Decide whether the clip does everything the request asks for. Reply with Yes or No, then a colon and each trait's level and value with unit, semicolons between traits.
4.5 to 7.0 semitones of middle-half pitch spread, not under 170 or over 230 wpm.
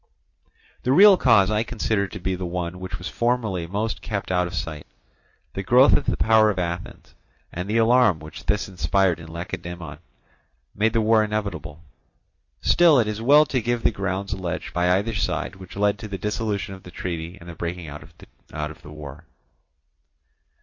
No: average, 4.0 semitones; average, 180 wpm